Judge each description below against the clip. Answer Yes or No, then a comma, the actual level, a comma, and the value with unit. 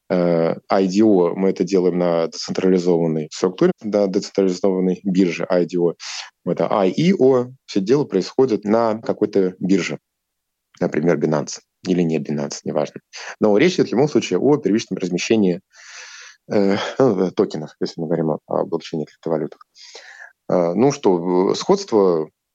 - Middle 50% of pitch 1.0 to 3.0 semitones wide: Yes, average, 2.7 semitones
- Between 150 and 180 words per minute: No, average, 120 wpm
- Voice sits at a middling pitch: No, very low, 95 Hz